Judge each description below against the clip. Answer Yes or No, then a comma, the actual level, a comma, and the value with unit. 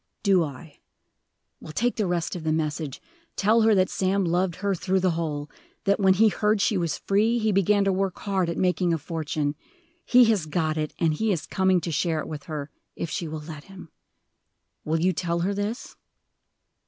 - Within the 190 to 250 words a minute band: Yes, fast, 205 wpm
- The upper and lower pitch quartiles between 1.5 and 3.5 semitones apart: No, average, 3.9 semitones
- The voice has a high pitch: No, medium, 180 Hz